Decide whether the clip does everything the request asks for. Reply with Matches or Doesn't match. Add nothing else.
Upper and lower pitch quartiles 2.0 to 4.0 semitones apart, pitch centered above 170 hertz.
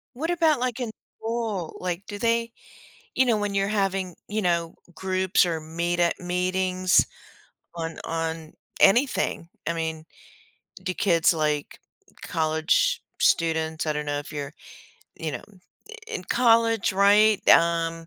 Doesn't match